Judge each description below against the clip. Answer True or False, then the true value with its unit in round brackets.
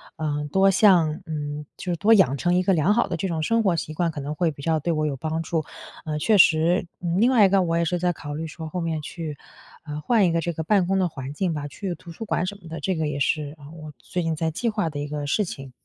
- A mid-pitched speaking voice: True (165 Hz)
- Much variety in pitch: False (3.3 semitones)